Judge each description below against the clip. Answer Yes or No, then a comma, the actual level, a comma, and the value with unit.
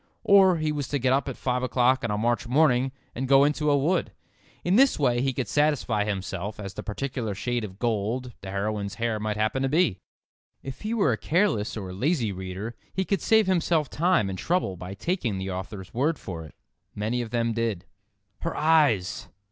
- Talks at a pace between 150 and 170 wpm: No, fast, 205 wpm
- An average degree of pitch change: No, wide, 6.2 semitones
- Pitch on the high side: No, low, 120 Hz